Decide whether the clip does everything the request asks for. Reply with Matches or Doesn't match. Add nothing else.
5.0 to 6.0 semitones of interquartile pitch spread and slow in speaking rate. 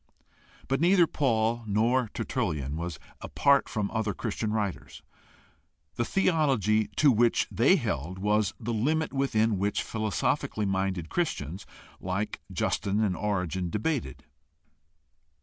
Doesn't match